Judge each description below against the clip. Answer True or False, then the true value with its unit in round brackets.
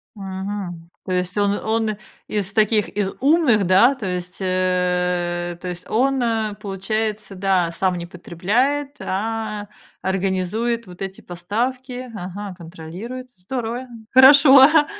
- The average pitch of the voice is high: True (205 Hz)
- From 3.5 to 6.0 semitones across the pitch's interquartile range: True (4.5 semitones)